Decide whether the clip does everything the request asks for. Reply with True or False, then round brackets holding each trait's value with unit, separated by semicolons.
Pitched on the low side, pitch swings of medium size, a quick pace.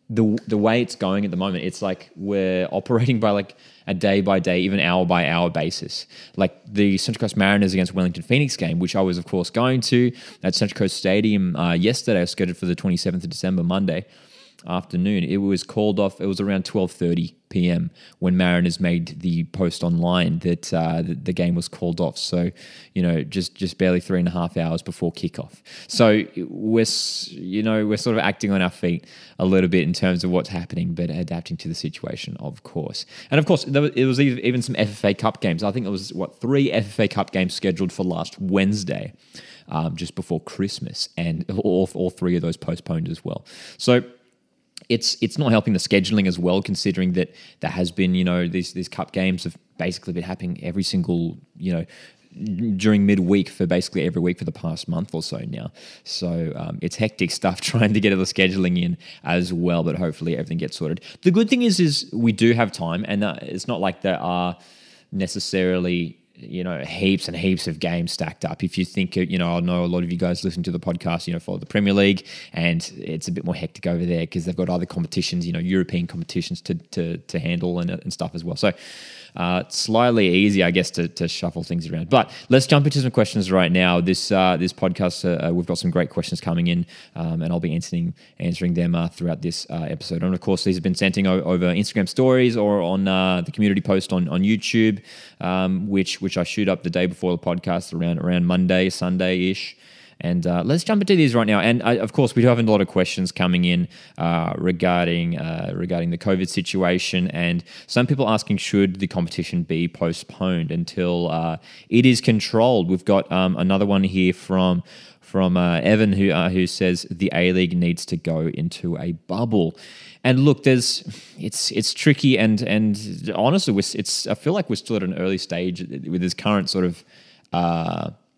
True (95 Hz; 4.1 semitones; 215 wpm)